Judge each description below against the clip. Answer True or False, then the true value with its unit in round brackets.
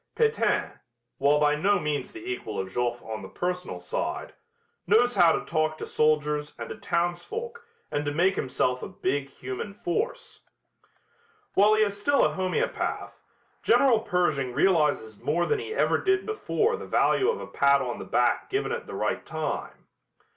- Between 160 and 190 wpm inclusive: True (170 wpm)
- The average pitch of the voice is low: False (175 Hz)